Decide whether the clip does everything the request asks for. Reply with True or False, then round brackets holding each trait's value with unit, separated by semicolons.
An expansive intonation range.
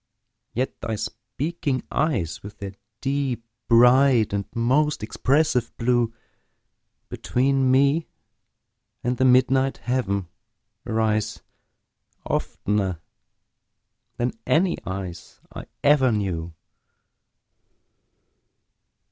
False (4.4 semitones)